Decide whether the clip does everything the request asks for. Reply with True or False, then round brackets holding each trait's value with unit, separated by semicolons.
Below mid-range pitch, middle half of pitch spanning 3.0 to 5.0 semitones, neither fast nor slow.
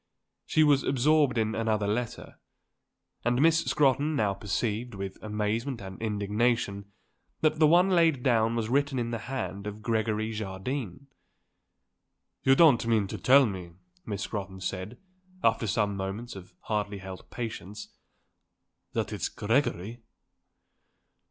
False (110 Hz; 4.3 semitones; 130 wpm)